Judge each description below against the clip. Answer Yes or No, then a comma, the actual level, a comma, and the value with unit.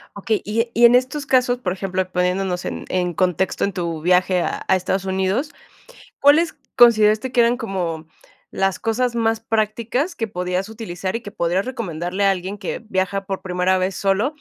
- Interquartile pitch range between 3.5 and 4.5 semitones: Yes, average, 4.1 semitones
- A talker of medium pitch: No, high, 195 Hz